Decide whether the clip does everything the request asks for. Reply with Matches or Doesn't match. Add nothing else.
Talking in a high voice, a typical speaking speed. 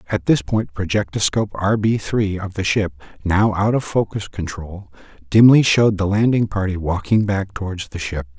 Doesn't match